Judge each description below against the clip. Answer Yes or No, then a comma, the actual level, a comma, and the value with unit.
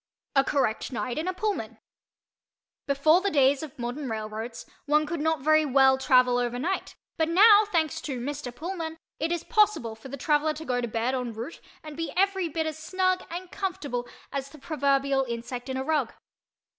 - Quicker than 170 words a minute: Yes, average, 190 wpm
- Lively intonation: No, average, 4.5 semitones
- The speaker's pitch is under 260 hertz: No, very high, 290 Hz